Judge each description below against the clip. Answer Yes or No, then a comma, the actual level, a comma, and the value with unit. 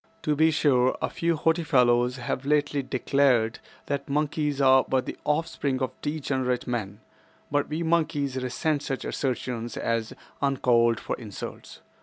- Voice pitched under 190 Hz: Yes, low, 135 Hz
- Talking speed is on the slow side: No, average, 145 wpm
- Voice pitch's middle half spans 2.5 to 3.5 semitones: Yes, average, 3.1 semitones